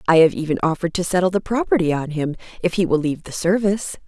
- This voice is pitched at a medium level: Yes, medium, 175 Hz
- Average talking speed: No, fast, 235 wpm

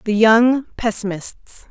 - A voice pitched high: Yes, high, 225 Hz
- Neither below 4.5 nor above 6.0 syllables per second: No, 4.3 syllables/s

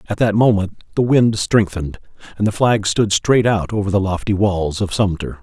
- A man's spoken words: Yes, male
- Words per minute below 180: No, average, 200 wpm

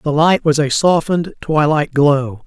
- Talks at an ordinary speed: Yes, average, 170 wpm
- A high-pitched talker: No, medium, 150 Hz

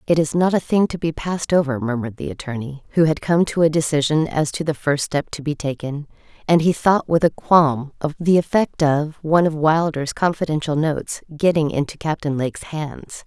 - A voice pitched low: No, medium, 155 Hz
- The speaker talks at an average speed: No, fast, 210 wpm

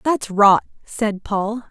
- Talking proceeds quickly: No, average, 140 wpm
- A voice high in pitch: Yes, high, 215 Hz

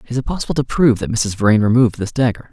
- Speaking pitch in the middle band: No, low, 115 Hz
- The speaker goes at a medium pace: No, fast, 260 wpm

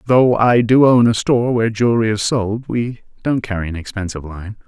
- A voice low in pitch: Yes, low, 110 Hz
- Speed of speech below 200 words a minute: No, fast, 205 wpm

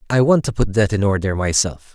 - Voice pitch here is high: No, low, 105 Hz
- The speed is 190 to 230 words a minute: No, fast, 245 wpm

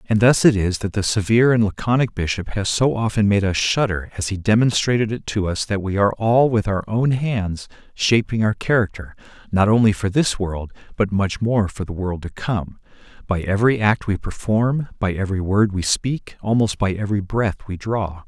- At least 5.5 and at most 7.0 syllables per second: No, 5.2 syllables/s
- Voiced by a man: Yes, male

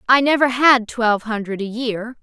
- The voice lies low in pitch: No, high, 235 Hz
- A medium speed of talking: Yes, average, 190 wpm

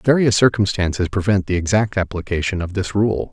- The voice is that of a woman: No, male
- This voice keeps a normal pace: Yes, average, 165 wpm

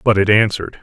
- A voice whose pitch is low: Yes, low, 105 Hz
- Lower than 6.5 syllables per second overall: No, 6.9 syllables/s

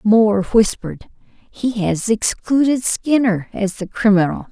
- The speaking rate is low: Yes, slow, 120 wpm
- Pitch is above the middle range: Yes, high, 215 Hz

